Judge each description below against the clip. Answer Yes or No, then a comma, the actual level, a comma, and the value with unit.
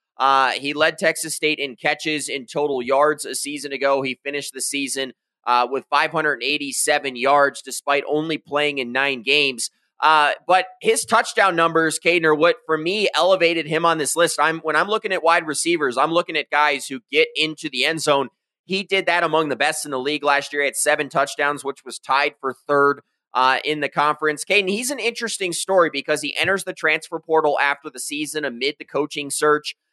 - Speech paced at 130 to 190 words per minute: No, fast, 205 wpm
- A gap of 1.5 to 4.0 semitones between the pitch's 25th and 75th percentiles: Yes, average, 2.8 semitones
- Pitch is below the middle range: No, medium, 150 Hz